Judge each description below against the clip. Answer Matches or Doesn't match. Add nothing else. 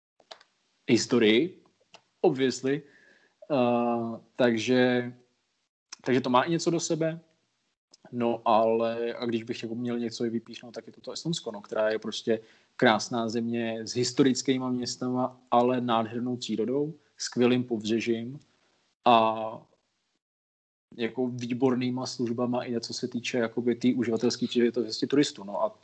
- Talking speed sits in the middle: Matches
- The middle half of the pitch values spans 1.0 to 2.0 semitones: Matches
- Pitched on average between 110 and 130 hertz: Matches